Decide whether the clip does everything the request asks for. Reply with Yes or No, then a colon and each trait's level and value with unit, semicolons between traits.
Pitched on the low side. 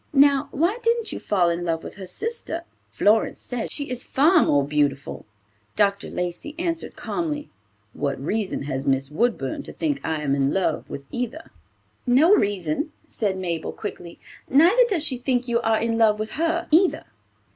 No: high, 230 Hz